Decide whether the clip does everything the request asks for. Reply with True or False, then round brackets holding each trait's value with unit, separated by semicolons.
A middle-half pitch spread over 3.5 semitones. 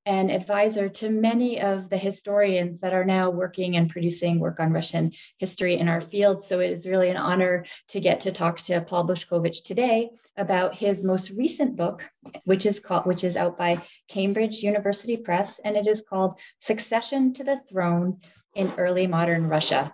False (2.7 semitones)